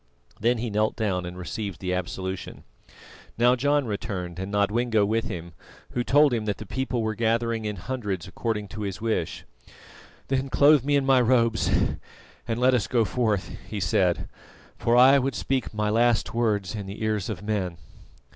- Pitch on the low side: Yes, low, 110 Hz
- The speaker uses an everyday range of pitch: Yes, average, 3.5 semitones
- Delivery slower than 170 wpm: No, average, 175 wpm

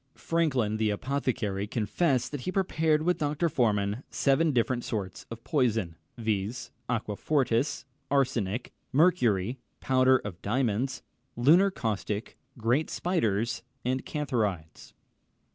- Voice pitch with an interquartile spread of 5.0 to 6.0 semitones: Yes, average, 5.3 semitones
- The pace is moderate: No, slow, 110 wpm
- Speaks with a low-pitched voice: Yes, low, 125 Hz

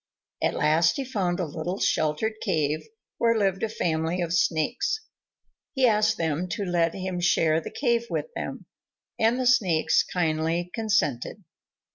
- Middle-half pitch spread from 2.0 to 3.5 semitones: No, average, 5.3 semitones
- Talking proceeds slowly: No, average, 150 wpm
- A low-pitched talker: No, medium, 180 Hz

